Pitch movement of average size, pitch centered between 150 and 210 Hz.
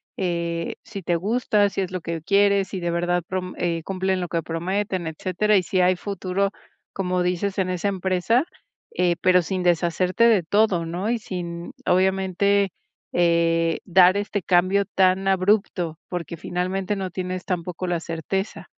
No: narrow, 2.1 semitones; medium, 185 Hz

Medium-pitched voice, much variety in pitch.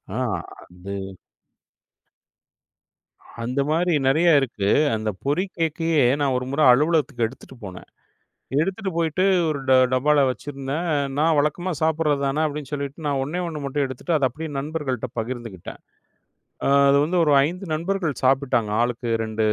No: medium, 145 Hz; average, 3.7 semitones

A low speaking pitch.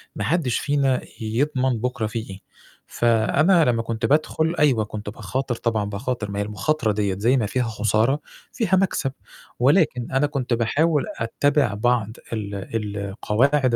Yes: low, 120 Hz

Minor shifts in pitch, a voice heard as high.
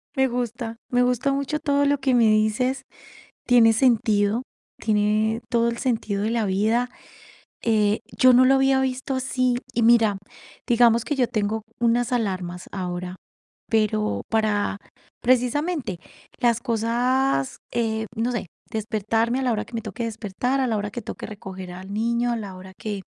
No: average, 3.0 semitones; high, 230 Hz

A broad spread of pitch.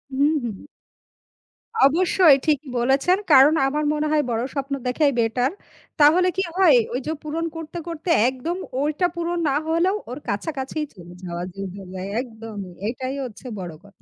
Yes: wide, 5.8 semitones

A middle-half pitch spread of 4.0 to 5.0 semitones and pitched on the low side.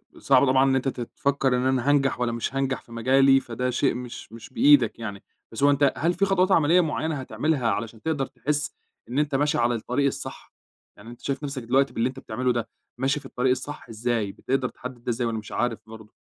No: average, 3.0 semitones; low, 130 Hz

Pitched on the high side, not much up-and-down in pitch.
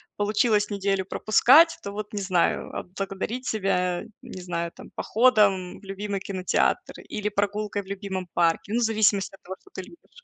Yes: high, 200 Hz; narrow, 2.1 semitones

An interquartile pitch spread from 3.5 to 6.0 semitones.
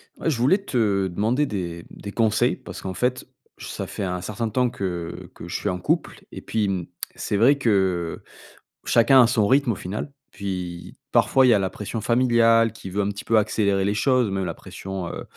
Yes: average, 3.8 semitones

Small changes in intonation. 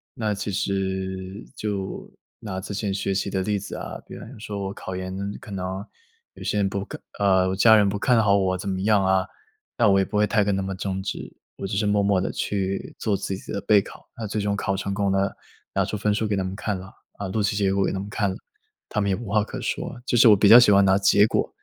Yes: narrow, 1.4 semitones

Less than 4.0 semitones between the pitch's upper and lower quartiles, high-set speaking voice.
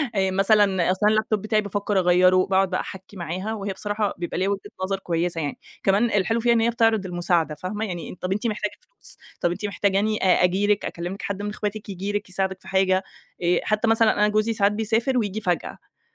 Yes: narrow, 2.4 semitones; high, 200 Hz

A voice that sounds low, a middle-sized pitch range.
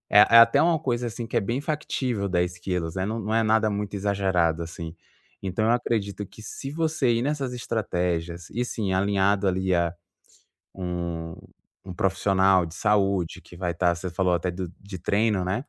Yes: very low, 95 Hz; average, 3.7 semitones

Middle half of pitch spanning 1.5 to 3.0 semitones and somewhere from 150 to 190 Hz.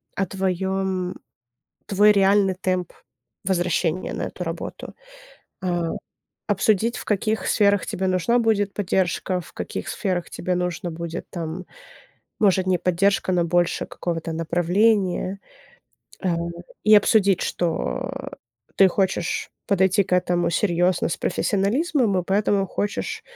Yes: narrow, 2.4 semitones; medium, 185 Hz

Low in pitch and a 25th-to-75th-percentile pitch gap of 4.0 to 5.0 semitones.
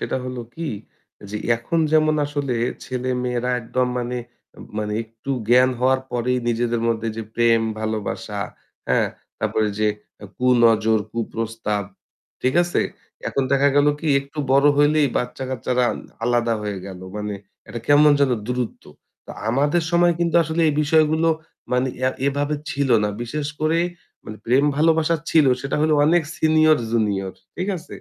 Yes: low, 125 Hz; average, 4.6 semitones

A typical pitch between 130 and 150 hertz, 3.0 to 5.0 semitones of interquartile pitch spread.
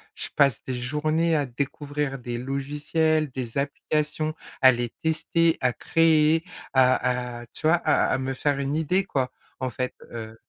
Yes: medium, 140 Hz; average, 3.5 semitones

